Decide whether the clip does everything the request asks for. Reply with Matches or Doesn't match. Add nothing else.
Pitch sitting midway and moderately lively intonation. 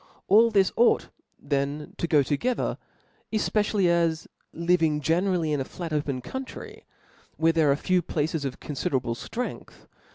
Matches